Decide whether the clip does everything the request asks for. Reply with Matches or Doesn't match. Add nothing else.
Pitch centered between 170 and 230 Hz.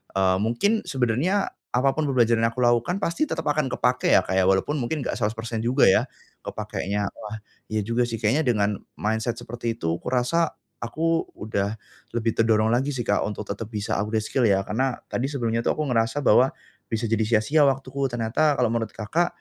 Doesn't match